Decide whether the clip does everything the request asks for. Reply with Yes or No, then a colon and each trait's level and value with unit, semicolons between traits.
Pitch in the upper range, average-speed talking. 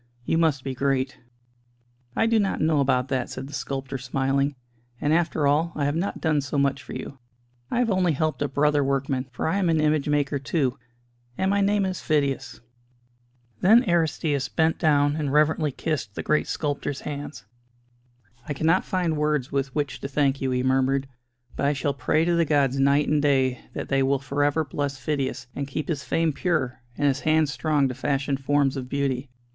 No: medium, 145 Hz; average, 195 wpm